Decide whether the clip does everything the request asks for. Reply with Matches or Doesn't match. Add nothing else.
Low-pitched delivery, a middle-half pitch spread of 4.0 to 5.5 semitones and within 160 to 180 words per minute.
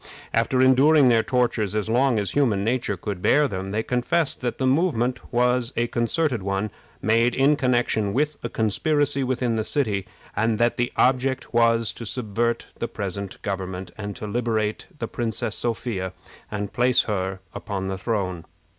Doesn't match